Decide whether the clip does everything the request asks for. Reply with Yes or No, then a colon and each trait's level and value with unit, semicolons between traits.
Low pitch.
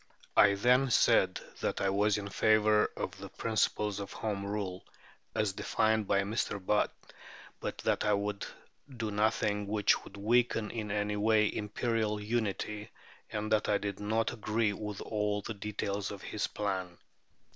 Yes: low, 105 Hz